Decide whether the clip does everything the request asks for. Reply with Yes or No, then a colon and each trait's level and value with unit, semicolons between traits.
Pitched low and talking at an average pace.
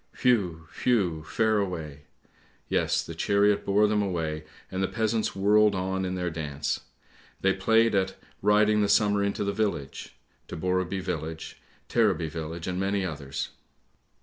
Yes: very low, 95 Hz; average, 150 wpm